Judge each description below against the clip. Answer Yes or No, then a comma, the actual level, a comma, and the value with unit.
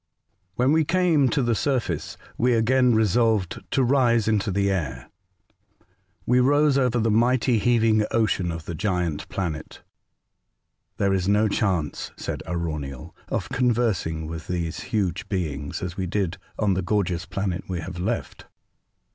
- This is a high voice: No, low, 105 Hz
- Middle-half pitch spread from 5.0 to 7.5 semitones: Yes, wide, 5.4 semitones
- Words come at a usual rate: Yes, average, 155 wpm